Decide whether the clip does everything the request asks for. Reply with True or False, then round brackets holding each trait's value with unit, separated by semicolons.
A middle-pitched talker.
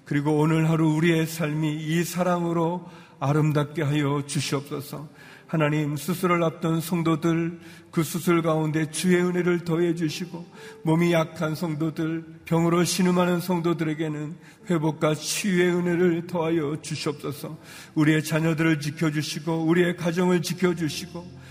True (165 Hz)